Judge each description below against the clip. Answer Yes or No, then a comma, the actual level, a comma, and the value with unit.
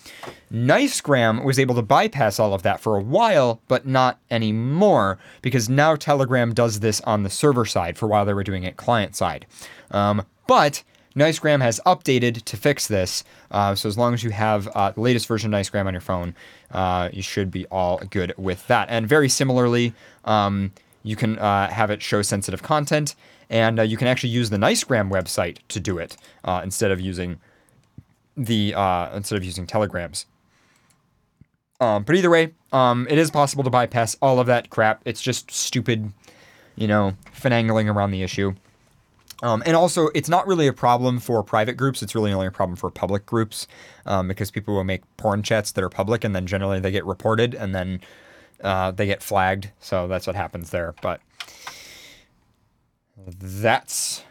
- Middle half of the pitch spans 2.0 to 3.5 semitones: No, average, 4.1 semitones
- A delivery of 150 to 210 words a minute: Yes, average, 185 wpm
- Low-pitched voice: Yes, low, 110 Hz